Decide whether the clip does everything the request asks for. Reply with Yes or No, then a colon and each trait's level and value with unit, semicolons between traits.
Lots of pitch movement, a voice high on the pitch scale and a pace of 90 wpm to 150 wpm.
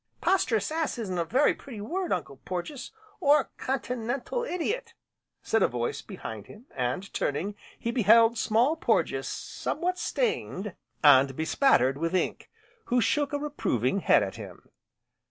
Yes: wide, 9.0 semitones; high, 230 Hz; average, 140 wpm